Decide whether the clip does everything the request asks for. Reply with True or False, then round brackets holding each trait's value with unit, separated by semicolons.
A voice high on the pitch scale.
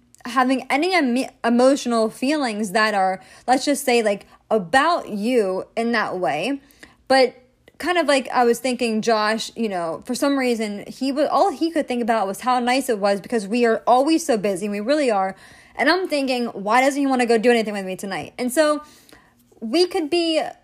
True (245 Hz)